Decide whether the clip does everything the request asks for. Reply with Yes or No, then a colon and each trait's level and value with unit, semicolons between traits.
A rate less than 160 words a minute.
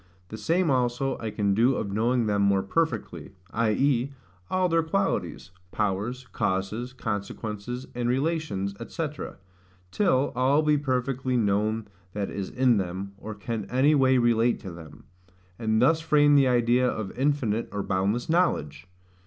Yes: average, 145 wpm